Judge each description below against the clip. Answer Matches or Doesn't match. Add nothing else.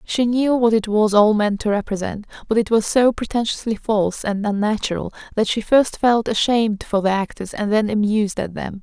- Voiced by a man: Doesn't match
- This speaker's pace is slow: Doesn't match